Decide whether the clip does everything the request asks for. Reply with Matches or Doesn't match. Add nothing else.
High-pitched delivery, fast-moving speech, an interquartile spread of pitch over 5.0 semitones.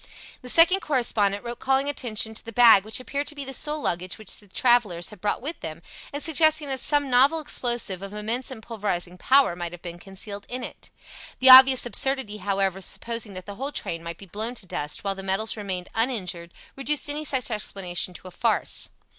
Matches